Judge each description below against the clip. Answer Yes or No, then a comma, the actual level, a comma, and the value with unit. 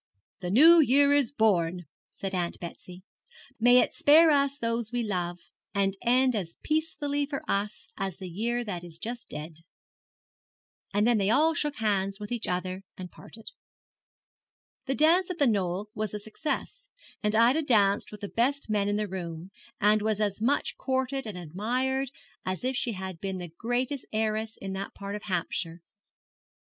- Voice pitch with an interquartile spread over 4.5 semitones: Yes, average, 5.3 semitones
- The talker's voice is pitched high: Yes, high, 215 Hz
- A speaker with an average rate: Yes, average, 175 wpm